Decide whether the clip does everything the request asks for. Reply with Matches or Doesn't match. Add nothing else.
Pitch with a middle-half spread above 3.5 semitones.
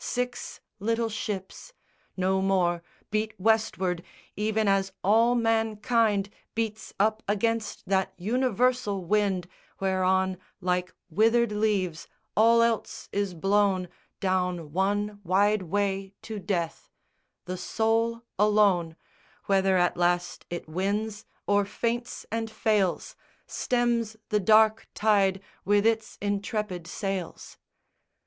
Doesn't match